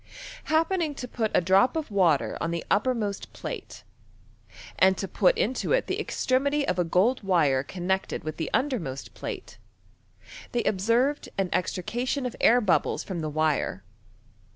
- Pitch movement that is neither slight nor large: No, wide, 6.6 semitones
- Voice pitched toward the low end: No, high, 200 Hz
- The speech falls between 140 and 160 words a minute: Yes, average, 155 wpm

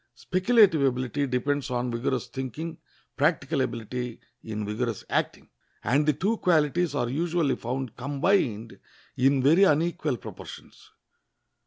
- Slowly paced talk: Yes, slow, 120 wpm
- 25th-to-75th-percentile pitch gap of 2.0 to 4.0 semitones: No, average, 4.7 semitones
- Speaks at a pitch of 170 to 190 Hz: No, low, 135 Hz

